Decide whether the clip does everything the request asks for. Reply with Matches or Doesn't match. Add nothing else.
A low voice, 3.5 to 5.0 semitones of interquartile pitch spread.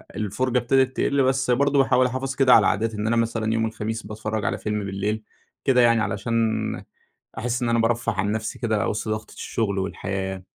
Doesn't match